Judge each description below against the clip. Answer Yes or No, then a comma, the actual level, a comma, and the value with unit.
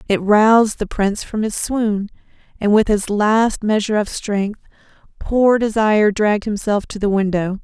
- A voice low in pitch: No, high, 210 Hz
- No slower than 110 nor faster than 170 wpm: Yes, average, 165 wpm